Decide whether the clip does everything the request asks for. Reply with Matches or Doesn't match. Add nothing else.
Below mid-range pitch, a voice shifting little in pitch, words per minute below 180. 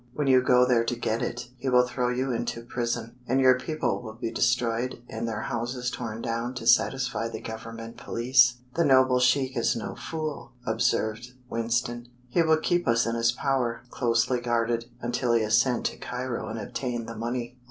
Doesn't match